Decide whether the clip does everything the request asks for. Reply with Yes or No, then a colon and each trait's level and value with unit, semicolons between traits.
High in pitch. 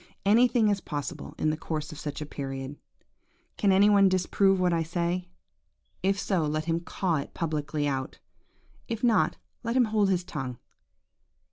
No: medium, 175 Hz